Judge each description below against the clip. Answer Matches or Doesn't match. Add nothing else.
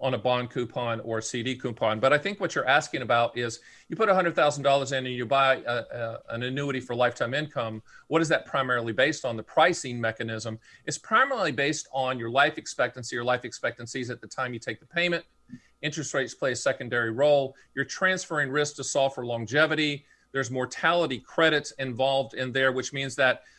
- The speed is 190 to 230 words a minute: Matches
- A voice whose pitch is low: Matches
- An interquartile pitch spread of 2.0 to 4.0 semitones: Matches